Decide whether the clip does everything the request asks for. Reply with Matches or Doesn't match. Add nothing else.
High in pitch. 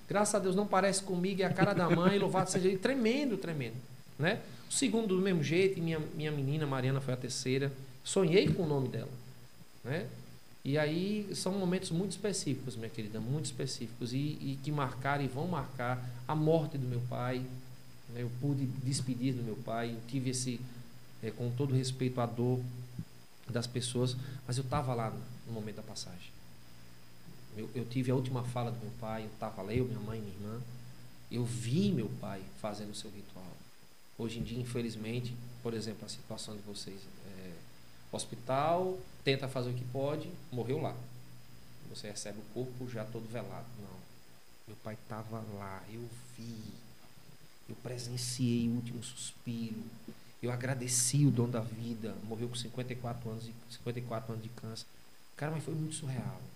Doesn't match